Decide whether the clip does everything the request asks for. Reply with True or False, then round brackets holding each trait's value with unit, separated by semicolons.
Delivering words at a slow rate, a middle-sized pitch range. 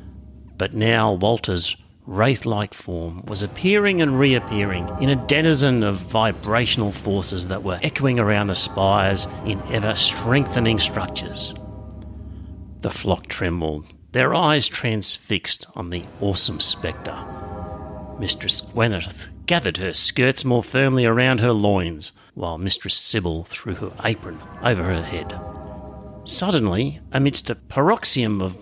True (120 wpm; 4.4 semitones)